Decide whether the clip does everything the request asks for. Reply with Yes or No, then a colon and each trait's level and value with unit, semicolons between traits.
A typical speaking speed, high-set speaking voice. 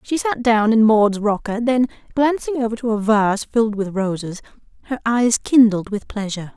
Yes: average, 185 wpm; high, 225 Hz